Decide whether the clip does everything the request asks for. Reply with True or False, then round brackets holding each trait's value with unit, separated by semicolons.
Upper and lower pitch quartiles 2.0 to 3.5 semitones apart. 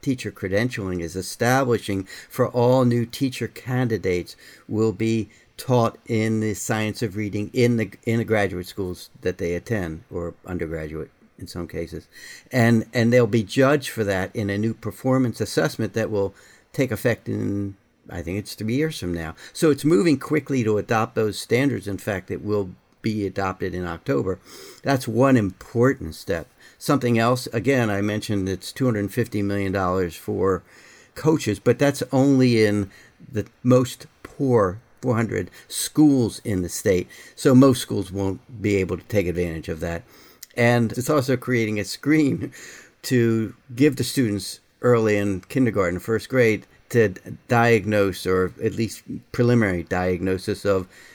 False (4.2 semitones)